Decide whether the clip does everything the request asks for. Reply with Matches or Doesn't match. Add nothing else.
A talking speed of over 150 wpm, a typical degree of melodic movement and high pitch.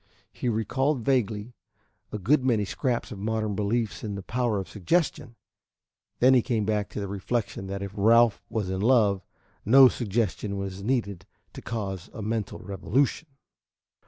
Doesn't match